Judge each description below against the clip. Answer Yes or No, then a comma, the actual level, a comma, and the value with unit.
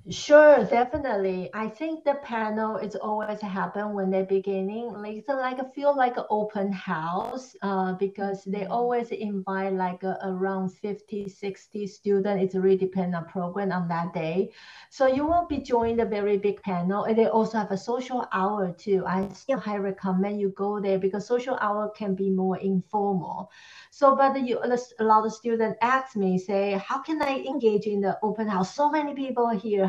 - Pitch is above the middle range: Yes, high, 205 Hz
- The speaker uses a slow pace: No, average, 185 wpm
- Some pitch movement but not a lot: Yes, average, 3.6 semitones